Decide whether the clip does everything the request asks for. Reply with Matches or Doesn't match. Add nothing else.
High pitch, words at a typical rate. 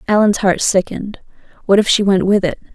Matches